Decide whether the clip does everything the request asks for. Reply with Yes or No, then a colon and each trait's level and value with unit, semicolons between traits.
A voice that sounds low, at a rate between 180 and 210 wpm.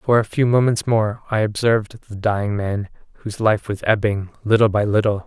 Yes: low, 105 Hz; average, 195 wpm